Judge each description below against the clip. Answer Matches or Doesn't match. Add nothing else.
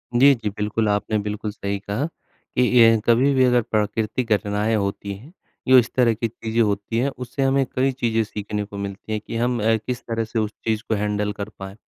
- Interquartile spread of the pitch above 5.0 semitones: Doesn't match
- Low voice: Matches